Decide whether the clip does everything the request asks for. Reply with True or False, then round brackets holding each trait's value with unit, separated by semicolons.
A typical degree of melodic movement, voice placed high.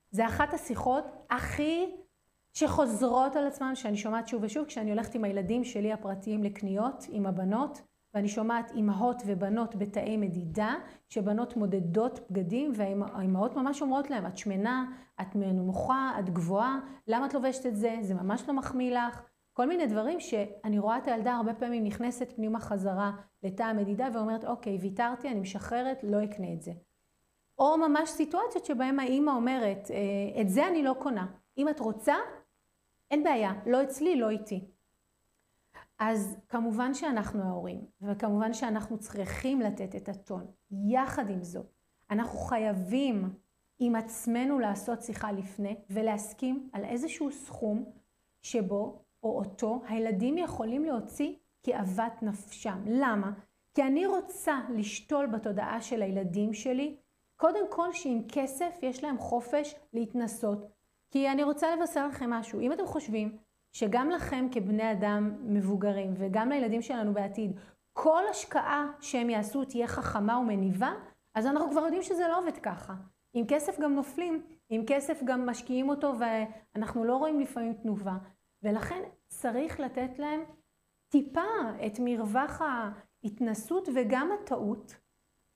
True (4.8 semitones; 235 Hz)